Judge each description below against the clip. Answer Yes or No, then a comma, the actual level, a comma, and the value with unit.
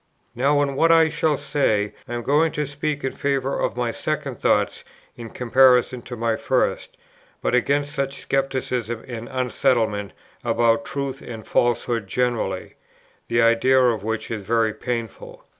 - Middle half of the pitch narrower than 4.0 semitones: Yes, average, 3.2 semitones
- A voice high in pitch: No, low, 125 Hz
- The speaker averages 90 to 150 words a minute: No, average, 160 wpm